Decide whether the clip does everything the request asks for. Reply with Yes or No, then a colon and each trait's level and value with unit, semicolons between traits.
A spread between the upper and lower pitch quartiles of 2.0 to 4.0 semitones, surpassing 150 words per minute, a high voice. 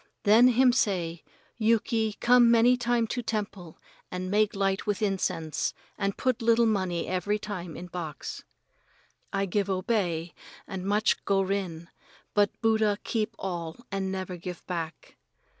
No: average, 3.6 semitones; average, 140 wpm; high, 200 Hz